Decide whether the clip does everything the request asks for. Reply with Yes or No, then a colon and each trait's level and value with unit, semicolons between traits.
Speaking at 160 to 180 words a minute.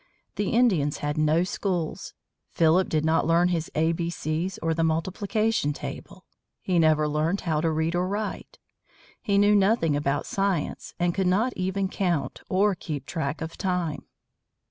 Yes: average, 165 wpm